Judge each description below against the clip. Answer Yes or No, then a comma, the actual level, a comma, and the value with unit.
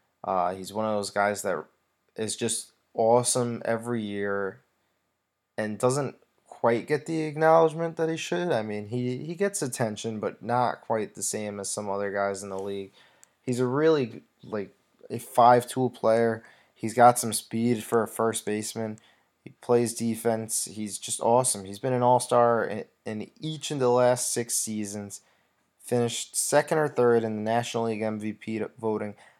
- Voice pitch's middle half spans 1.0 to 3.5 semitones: Yes, average, 2.8 semitones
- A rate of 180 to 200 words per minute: No, average, 170 wpm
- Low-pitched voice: Yes, low, 115 Hz